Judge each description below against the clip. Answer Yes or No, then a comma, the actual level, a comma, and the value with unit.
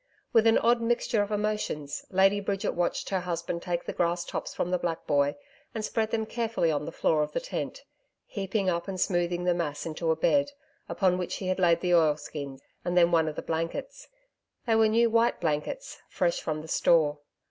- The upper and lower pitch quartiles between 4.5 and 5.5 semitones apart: Yes, average, 4.8 semitones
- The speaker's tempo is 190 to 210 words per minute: Yes, average, 200 wpm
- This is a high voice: No, medium, 180 Hz